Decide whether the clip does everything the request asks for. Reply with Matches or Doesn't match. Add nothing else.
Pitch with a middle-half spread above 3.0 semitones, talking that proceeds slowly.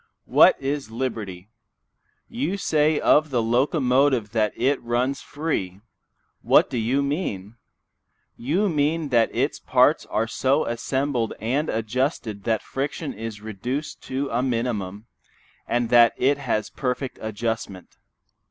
Matches